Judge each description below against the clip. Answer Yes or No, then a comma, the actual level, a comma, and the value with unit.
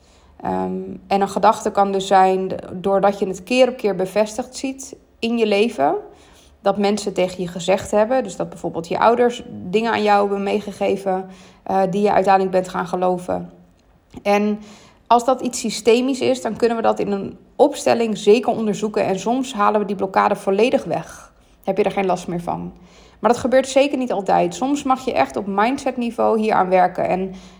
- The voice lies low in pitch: No, high, 205 Hz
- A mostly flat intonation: No, average, 3.7 semitones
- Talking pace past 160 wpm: Yes, average, 190 wpm